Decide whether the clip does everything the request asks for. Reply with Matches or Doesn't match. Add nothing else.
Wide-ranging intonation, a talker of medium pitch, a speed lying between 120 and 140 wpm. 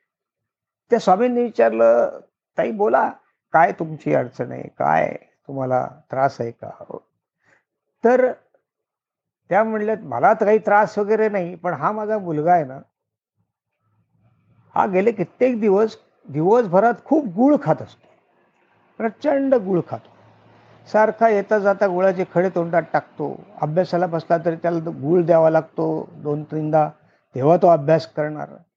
Matches